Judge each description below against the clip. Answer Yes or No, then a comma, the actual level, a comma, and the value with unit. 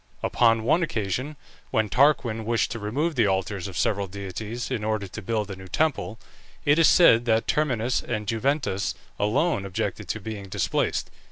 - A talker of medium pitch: No, low, 110 Hz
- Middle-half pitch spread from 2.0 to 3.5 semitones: No, average, 4.1 semitones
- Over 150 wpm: Yes, average, 170 wpm